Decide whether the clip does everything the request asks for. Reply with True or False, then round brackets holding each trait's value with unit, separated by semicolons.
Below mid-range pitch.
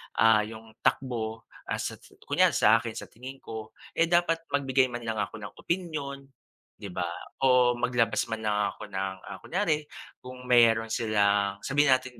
True (120 Hz)